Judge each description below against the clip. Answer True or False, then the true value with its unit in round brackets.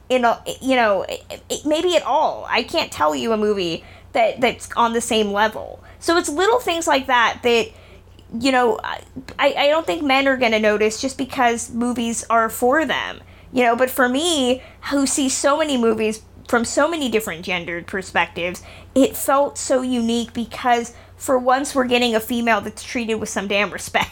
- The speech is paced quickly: False (185 wpm)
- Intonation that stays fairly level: False (3.7 semitones)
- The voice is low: False (245 Hz)